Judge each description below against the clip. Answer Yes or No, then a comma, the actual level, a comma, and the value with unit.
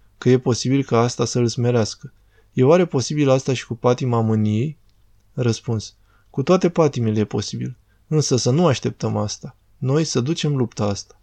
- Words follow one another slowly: No, fast, 170 wpm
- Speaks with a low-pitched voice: Yes, low, 120 Hz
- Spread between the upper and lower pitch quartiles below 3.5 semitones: No, average, 4.1 semitones